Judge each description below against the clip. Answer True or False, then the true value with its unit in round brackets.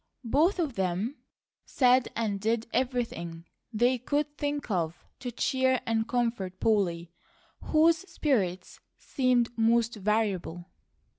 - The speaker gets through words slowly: True (115 wpm)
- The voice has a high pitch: True (230 Hz)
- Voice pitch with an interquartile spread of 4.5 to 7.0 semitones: True (4.9 semitones)